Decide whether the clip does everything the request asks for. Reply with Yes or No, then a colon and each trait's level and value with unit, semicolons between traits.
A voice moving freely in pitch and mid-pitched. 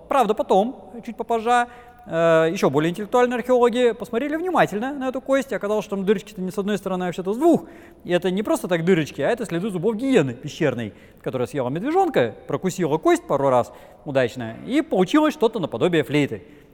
No: wide, 6.8 semitones; high, 210 Hz